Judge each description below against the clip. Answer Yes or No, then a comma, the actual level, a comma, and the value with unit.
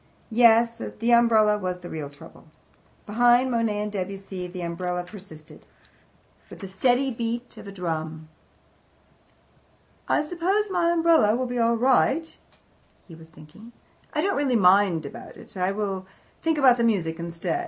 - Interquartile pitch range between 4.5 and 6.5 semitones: Yes, average, 5.2 semitones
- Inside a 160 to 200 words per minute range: No, average, 150 wpm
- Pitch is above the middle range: Yes, high, 210 Hz